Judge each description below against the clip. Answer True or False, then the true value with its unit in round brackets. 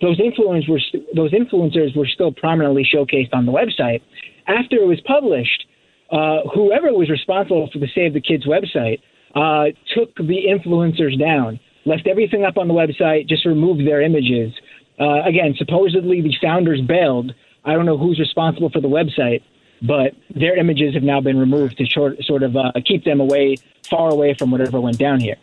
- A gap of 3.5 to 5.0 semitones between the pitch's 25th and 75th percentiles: True (3.8 semitones)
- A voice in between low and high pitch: True (155 Hz)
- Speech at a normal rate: True (185 wpm)